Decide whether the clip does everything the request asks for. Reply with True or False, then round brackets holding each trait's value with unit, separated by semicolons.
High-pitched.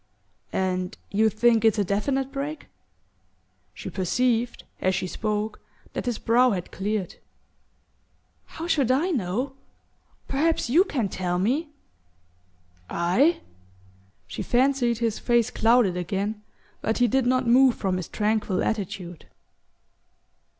True (225 Hz)